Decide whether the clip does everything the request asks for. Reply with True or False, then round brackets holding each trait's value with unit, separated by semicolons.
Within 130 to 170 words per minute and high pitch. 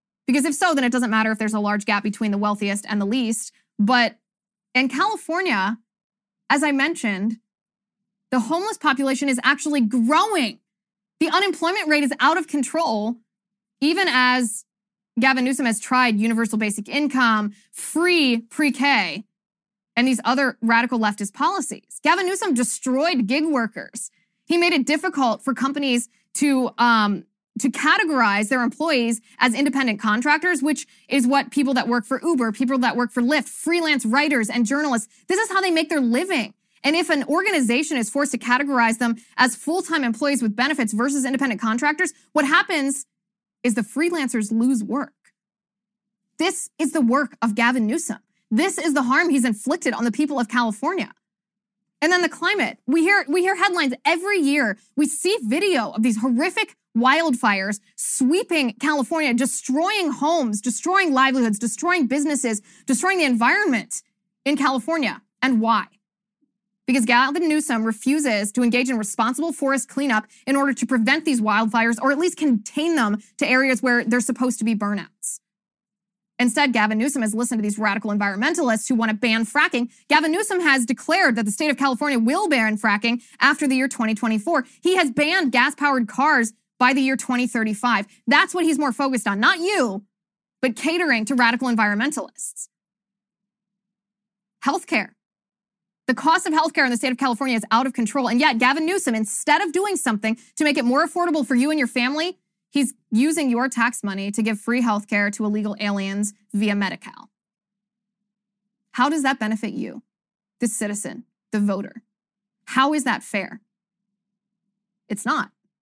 True (165 wpm; 245 Hz)